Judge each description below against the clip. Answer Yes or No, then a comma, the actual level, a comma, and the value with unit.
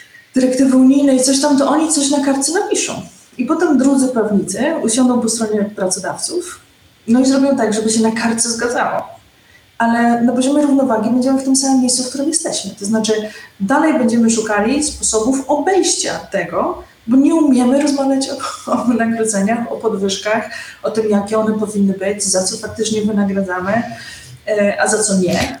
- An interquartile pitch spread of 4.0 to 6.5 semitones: Yes, average, 4.3 semitones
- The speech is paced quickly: Yes, fast, 165 wpm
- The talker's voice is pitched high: Yes, high, 235 Hz